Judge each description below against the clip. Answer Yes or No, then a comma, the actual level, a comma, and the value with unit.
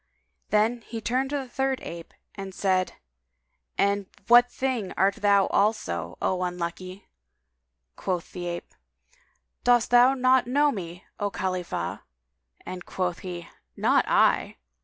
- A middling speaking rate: No, slow, 130 wpm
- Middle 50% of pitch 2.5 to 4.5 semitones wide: No, average, 5.1 semitones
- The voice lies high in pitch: Yes, high, 200 Hz